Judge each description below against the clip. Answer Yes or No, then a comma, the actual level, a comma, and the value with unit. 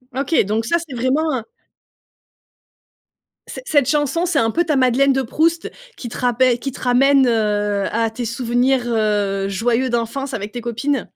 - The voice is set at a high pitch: Yes, high, 245 Hz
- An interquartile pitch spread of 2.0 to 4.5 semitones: Yes, average, 3.5 semitones